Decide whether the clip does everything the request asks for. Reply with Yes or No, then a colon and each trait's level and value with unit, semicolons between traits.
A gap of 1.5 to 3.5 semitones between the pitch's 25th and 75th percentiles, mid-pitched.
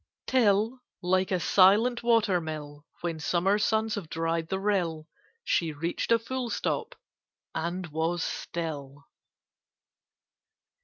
No: average, 4.7 semitones; medium, 180 Hz